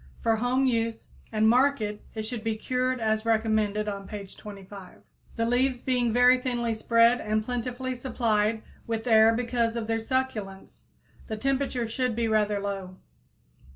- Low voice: No, high, 225 Hz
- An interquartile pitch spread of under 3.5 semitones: Yes, narrow, 2.4 semitones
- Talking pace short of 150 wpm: No, average, 155 wpm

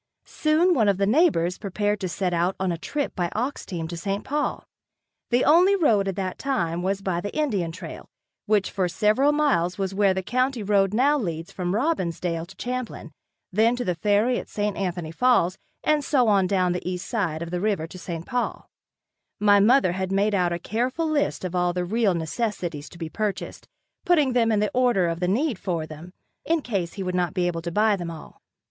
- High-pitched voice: Yes, high, 195 Hz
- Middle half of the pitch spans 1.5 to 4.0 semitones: No, wide, 5.5 semitones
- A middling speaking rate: No, fast, 210 wpm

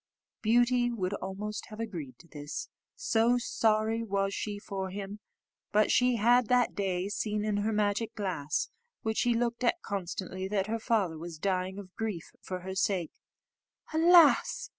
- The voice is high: Yes, high, 205 Hz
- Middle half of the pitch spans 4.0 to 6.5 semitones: No, average, 3.2 semitones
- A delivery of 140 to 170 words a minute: Yes, average, 160 wpm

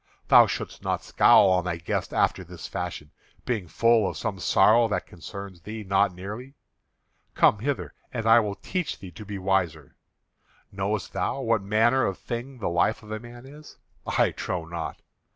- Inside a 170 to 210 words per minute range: Yes, average, 175 wpm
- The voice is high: No, low, 105 Hz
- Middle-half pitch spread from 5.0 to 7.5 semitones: No, average, 4.1 semitones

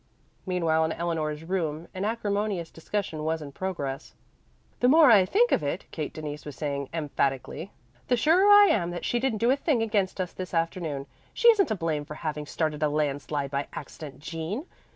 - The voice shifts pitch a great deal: Yes, wide, 5.8 semitones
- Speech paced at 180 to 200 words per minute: Yes, average, 190 wpm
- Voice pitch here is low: No, medium, 165 Hz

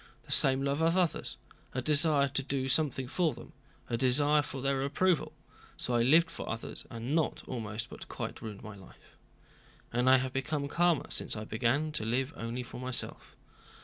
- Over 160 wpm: Yes, average, 180 wpm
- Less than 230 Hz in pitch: Yes, low, 135 Hz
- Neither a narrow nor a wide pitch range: Yes, average, 3.8 semitones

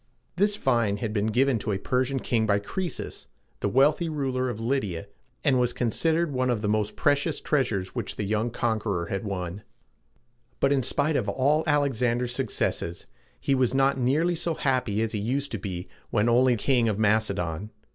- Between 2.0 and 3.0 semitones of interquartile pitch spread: No, average, 4.6 semitones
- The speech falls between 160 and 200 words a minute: Yes, average, 185 wpm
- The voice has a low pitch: Yes, low, 120 Hz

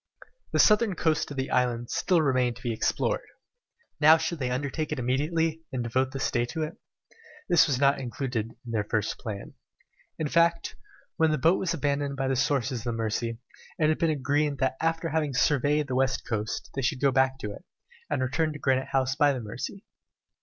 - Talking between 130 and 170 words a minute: No, fast, 205 wpm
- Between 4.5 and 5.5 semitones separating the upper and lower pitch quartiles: No, average, 3.8 semitones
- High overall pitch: No, low, 135 Hz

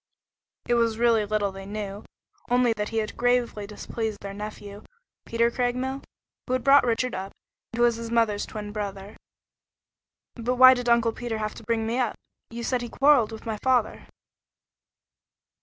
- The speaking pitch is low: No, high, 230 Hz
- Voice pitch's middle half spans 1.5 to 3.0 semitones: Yes, narrow, 2.6 semitones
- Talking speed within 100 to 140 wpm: No, average, 175 wpm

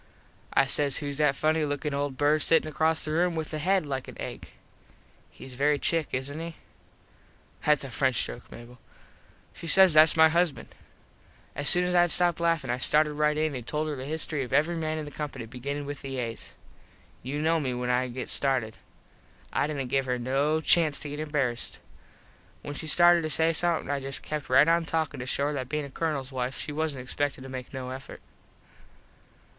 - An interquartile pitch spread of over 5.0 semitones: No, average, 3.0 semitones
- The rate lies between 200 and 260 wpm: Yes, fast, 205 wpm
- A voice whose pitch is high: No, medium, 145 Hz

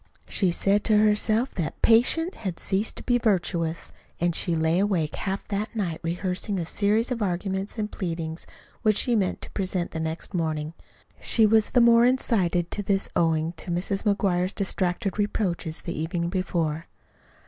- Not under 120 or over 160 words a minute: No, average, 170 wpm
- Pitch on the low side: No, high, 190 Hz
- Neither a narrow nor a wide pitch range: Yes, average, 3.8 semitones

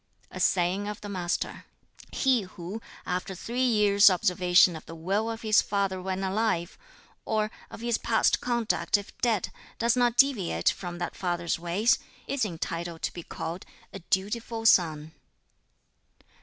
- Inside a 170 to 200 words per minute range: No, average, 150 wpm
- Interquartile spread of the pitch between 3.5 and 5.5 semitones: Yes, average, 4.2 semitones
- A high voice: Yes, high, 195 Hz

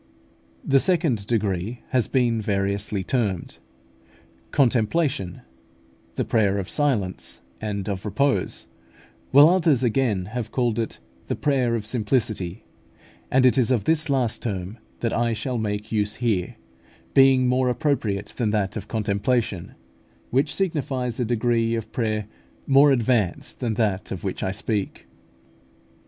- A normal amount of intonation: Yes, average, 3.9 semitones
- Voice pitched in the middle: No, low, 115 Hz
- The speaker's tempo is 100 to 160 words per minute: Yes, slow, 135 wpm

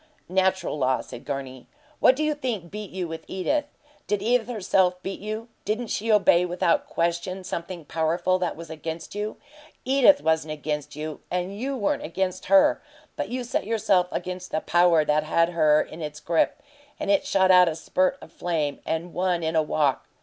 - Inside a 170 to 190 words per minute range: Yes, average, 185 wpm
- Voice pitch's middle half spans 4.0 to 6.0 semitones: Yes, average, 4.3 semitones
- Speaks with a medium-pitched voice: Yes, medium, 180 Hz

